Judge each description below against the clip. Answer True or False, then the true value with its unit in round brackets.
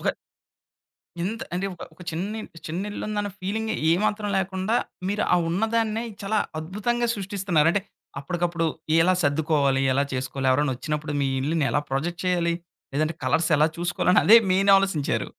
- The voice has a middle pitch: True (175 Hz)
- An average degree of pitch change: True (4.9 semitones)